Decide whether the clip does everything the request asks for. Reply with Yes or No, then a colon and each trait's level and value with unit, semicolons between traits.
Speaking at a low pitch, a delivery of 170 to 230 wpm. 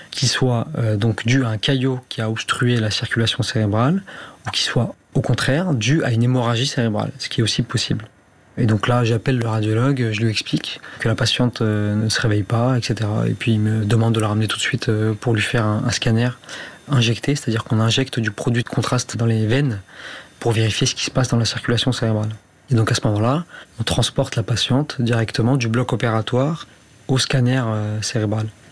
Yes: low, 115 Hz; average, 215 wpm